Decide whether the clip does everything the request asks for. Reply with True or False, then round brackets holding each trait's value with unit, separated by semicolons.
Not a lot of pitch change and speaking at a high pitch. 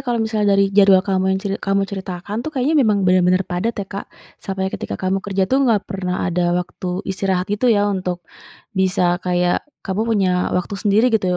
True (2.1 semitones; 195 Hz)